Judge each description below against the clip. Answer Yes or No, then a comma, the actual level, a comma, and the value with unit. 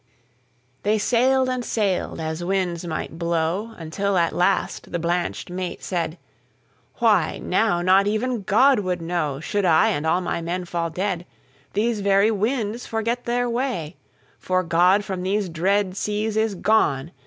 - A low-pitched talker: No, high, 190 Hz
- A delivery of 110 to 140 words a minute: Yes, slow, 135 wpm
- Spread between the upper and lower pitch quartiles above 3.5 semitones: Yes, average, 4.0 semitones